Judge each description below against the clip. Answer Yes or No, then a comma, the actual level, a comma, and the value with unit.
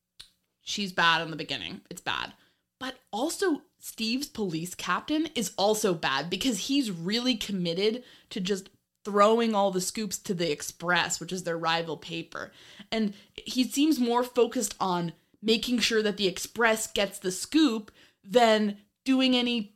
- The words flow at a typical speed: Yes, average, 150 wpm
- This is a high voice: Yes, high, 205 Hz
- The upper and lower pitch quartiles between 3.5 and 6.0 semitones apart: Yes, average, 5.1 semitones